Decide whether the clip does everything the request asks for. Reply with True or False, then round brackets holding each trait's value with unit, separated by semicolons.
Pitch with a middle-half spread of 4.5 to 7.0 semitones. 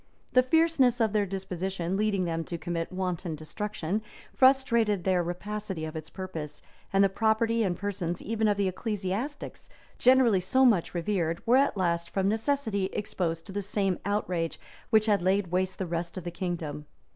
False (3.8 semitones)